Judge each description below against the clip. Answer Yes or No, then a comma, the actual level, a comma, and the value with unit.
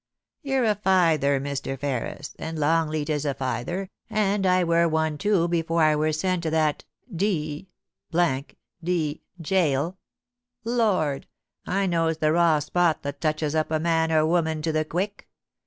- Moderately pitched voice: Yes, medium, 160 Hz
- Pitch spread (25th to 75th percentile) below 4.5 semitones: Yes, average, 2.9 semitones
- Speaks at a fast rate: No, average, 150 wpm